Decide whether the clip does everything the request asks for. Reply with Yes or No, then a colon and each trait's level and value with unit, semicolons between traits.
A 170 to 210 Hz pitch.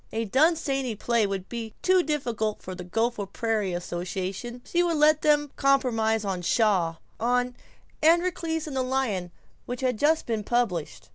No: high, 240 Hz